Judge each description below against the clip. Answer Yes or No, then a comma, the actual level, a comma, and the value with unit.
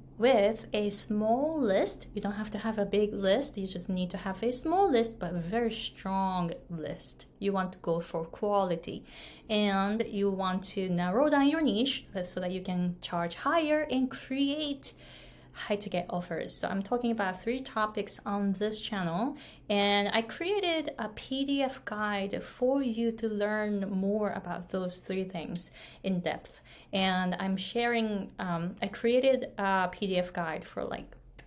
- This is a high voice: Yes, high, 205 Hz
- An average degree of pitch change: Yes, average, 4.0 semitones